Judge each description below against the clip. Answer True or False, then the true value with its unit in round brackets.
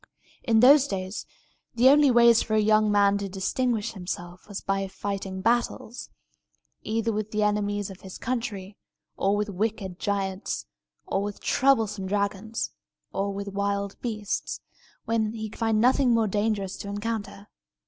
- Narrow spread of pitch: True (2.2 semitones)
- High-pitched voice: True (205 Hz)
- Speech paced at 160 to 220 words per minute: False (150 wpm)